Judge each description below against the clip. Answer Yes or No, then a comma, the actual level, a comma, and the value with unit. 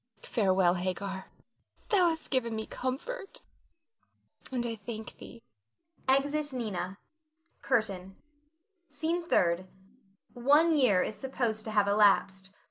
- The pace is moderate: No, slow, 110 wpm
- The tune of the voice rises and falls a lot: Yes, wide, 6.1 semitones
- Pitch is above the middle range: Yes, high, 225 Hz